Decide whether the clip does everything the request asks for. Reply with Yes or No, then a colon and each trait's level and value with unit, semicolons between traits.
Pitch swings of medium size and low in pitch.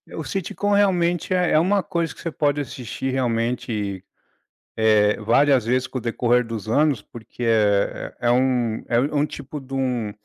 Yes: average, 4.8 semitones; low, 125 Hz